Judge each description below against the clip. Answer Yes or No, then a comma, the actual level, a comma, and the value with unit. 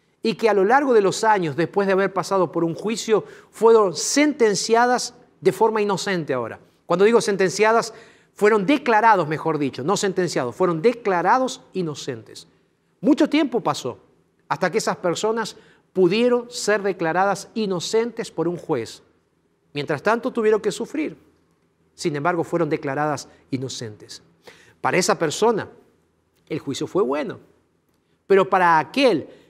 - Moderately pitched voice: No, high, 200 Hz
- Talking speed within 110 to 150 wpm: Yes, average, 135 wpm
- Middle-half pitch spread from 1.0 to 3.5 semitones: No, average, 4.8 semitones